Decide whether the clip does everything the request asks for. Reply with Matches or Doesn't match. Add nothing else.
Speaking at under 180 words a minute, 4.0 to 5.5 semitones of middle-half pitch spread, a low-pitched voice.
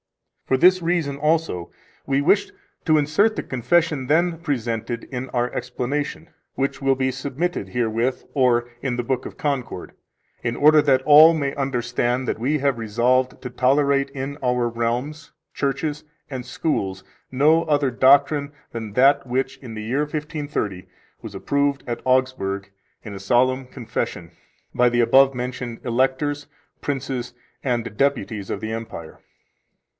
Doesn't match